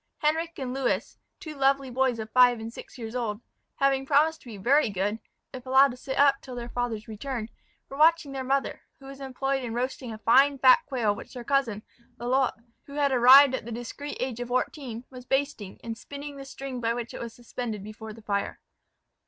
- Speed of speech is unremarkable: No, fast, 210 wpm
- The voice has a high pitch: Yes, very high, 255 Hz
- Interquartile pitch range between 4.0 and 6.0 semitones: No, average, 2.9 semitones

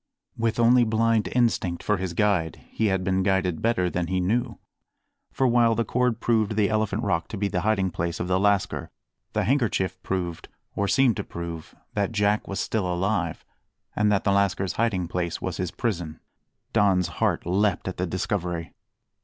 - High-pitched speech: No, low, 100 Hz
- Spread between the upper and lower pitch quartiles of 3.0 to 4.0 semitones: Yes, average, 3.3 semitones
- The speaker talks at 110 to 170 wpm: No, average, 180 wpm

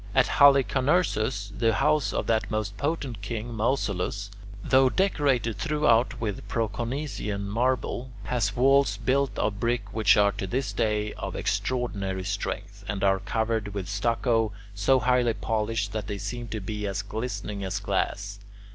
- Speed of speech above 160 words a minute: No, average, 145 wpm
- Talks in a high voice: No, low, 110 Hz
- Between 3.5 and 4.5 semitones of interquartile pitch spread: Yes, average, 3.8 semitones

